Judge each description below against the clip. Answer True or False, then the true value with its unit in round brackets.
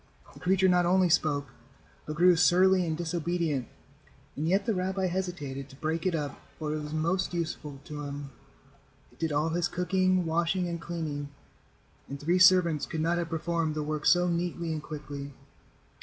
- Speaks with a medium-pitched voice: True (165 Hz)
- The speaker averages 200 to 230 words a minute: False (175 wpm)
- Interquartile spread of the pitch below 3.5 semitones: True (2.9 semitones)